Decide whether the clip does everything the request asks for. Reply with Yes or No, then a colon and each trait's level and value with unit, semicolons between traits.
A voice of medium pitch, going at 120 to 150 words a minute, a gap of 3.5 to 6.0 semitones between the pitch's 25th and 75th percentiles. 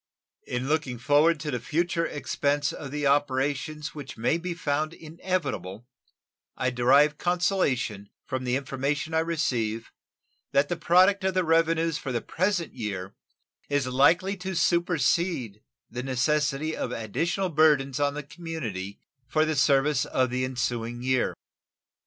Yes: medium, 145 Hz; average, 140 wpm; average, 4.4 semitones